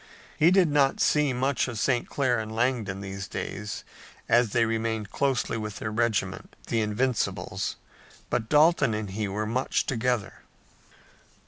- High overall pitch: No, low, 115 Hz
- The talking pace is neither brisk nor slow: Yes, average, 145 wpm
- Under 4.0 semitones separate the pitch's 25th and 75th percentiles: Yes, average, 3.6 semitones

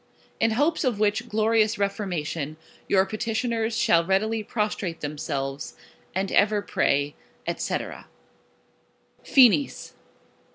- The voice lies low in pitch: No, high, 210 Hz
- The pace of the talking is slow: Yes, slow, 95 wpm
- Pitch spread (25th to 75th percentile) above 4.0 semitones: Yes, average, 4.9 semitones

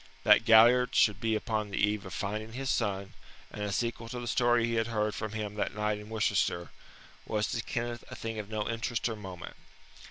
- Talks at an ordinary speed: No, fast, 215 wpm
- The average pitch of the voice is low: Yes, low, 110 Hz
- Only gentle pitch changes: Yes, narrow, 1.9 semitones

